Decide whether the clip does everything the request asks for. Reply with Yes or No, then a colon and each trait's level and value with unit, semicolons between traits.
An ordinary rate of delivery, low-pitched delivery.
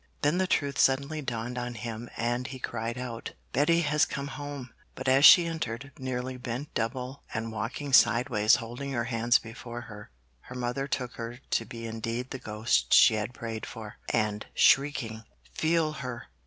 Yes: average, 170 wpm; low, 125 Hz